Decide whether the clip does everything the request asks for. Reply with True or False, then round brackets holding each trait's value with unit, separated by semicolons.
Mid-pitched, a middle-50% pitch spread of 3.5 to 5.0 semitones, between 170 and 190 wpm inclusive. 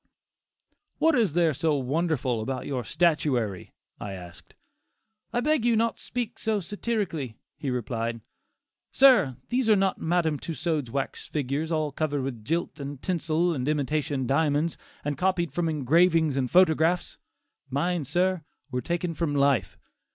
False (155 Hz; 4.5 semitones; 145 wpm)